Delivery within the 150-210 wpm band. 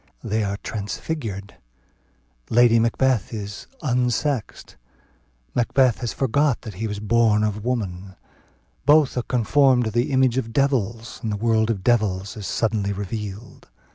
No: average, 140 wpm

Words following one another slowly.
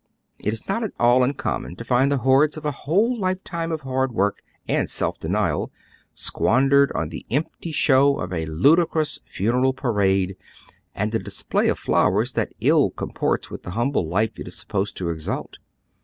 No: average, 180 wpm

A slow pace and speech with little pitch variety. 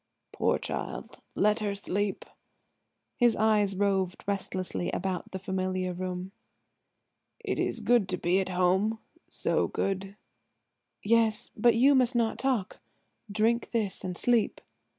No: slow, 120 wpm; average, 3.2 semitones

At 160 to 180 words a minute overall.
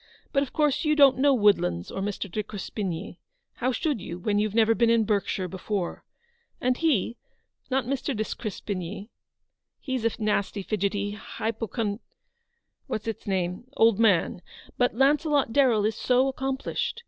Yes: average, 165 wpm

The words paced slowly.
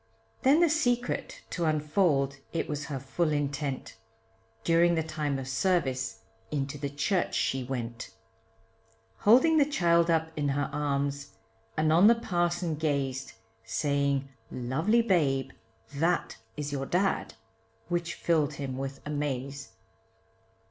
Yes: slow, 130 wpm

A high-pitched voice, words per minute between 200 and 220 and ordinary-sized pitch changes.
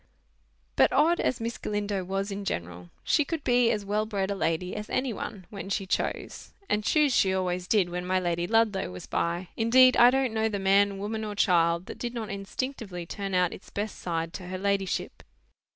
Yes: high, 200 Hz; fast, 205 wpm; average, 3.5 semitones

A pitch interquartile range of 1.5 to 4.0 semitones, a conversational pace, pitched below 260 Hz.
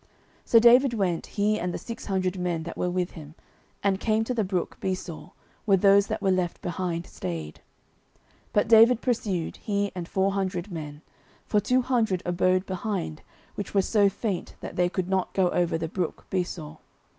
Yes: average, 2.9 semitones; average, 190 wpm; medium, 185 Hz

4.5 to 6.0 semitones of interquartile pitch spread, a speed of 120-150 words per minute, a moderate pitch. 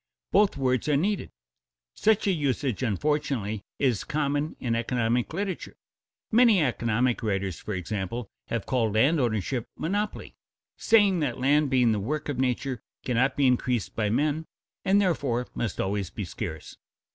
No: average, 5.1 semitones; average, 145 wpm; low, 130 Hz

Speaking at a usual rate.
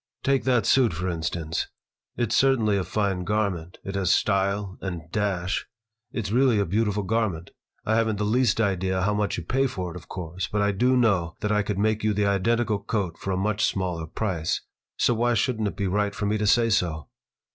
No: fast, 210 wpm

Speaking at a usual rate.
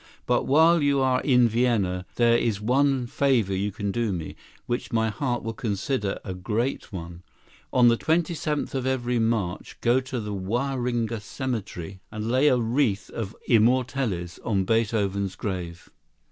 Yes: average, 160 wpm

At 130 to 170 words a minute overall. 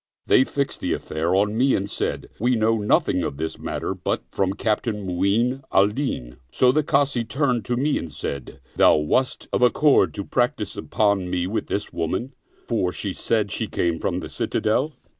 No: average, 195 wpm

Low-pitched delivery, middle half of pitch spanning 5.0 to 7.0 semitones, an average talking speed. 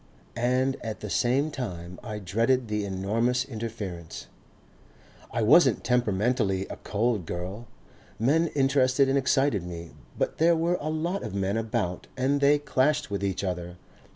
Yes: low, 115 Hz; wide, 5.5 semitones; average, 150 wpm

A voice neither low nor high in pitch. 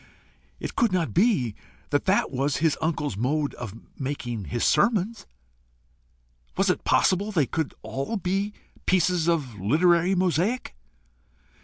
Yes: medium, 165 Hz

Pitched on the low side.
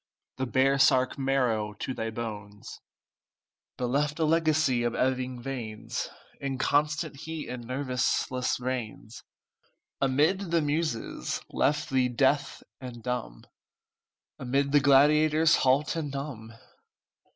Yes: low, 130 Hz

